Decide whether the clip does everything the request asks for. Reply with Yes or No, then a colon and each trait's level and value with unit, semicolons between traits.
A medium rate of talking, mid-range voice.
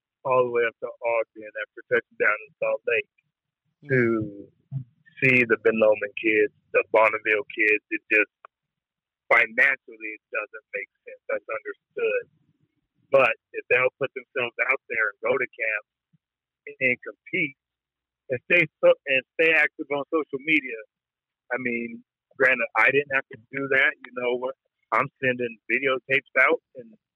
Yes: average, 155 wpm; medium, 180 Hz